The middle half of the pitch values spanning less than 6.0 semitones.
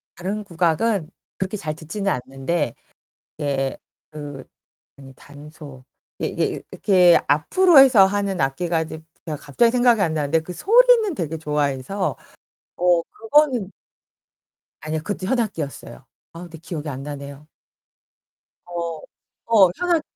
Yes: wide, 5.6 semitones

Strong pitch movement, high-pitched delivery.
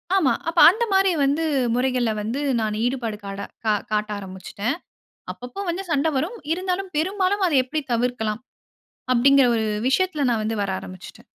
Yes: wide, 8.4 semitones; very high, 265 Hz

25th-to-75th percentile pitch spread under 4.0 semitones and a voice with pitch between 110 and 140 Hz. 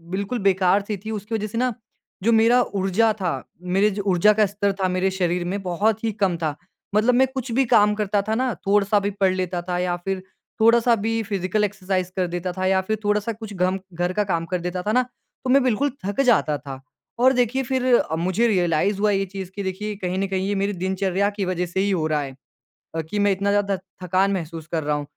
No: narrow, 2.6 semitones; high, 195 Hz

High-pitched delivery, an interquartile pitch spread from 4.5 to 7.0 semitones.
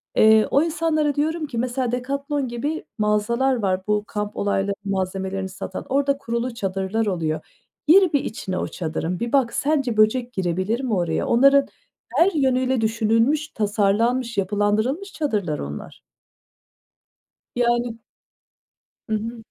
Yes: high, 230 Hz; average, 5.0 semitones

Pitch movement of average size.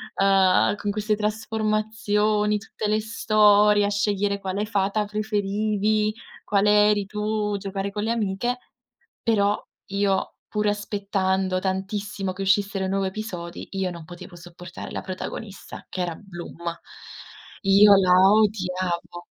No: narrow, 1.7 semitones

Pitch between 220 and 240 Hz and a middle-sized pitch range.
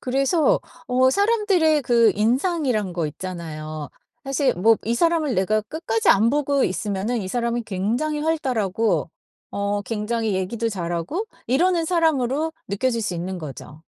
No: high, 230 Hz; wide, 7.2 semitones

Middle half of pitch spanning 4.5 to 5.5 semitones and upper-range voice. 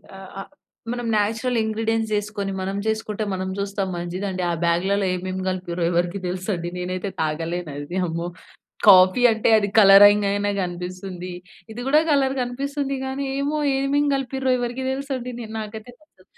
Yes: average, 5.0 semitones; high, 205 Hz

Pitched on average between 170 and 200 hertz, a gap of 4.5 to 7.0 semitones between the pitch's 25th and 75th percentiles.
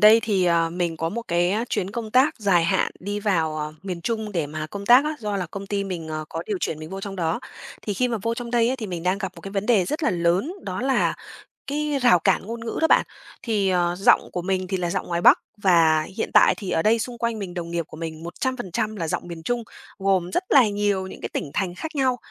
Yes: high, 195 Hz; average, 4.9 semitones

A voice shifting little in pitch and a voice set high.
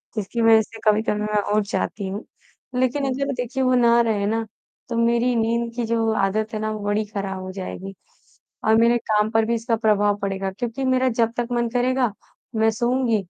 Yes: narrow, 2.3 semitones; high, 225 Hz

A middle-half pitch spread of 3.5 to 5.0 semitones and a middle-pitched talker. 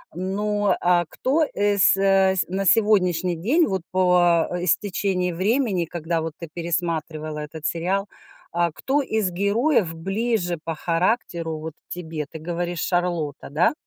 No: average, 3.1 semitones; medium, 180 Hz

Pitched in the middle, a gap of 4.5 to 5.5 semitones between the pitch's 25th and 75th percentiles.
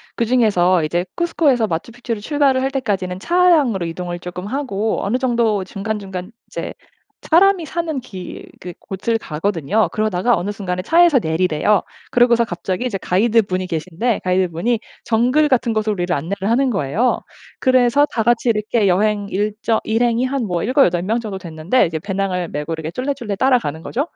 No: high, 215 Hz; average, 5.2 semitones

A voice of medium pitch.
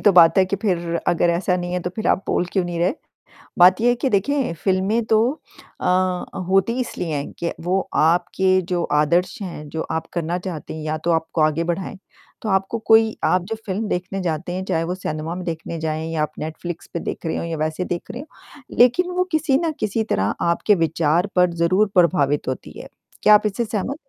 Yes: medium, 180 Hz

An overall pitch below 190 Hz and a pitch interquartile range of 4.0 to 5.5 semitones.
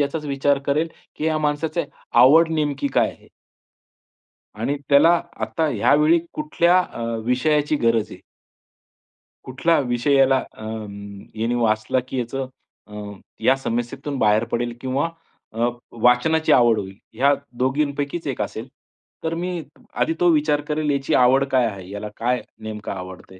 Yes: low, 135 Hz; average, 4.4 semitones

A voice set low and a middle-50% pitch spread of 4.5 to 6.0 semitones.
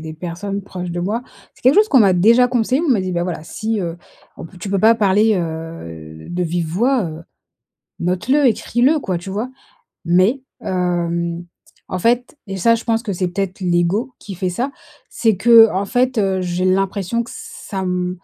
No: high, 190 Hz; average, 4.8 semitones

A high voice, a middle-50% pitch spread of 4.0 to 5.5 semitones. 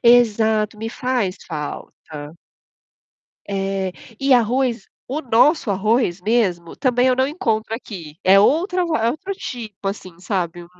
Yes: high, 220 Hz; average, 4.9 semitones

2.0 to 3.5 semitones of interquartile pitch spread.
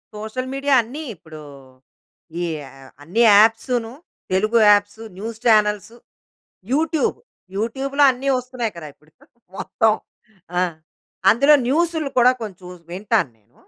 No: average, 4.4 semitones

